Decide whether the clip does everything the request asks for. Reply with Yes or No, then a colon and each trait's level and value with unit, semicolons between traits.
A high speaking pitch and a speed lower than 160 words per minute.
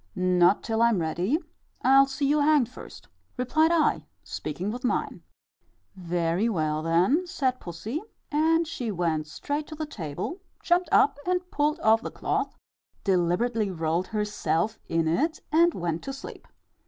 Yes: high, 225 Hz; average, 150 wpm